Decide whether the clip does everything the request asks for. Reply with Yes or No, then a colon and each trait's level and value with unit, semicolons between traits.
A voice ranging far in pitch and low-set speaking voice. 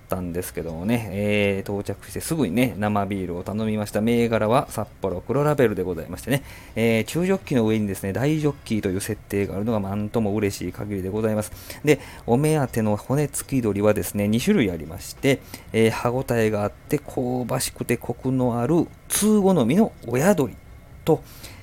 No: average, 4.5 semitones; low, 110 Hz